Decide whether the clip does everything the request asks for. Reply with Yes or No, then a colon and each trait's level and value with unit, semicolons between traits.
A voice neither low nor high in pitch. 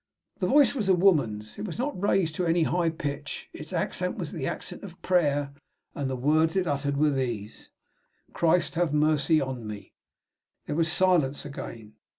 Yes: medium, 155 Hz